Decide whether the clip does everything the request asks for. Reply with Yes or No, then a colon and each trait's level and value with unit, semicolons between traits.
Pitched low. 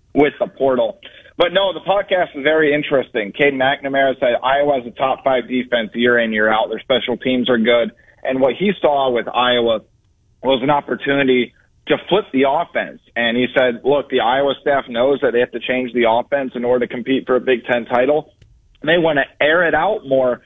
Yes: low, 125 Hz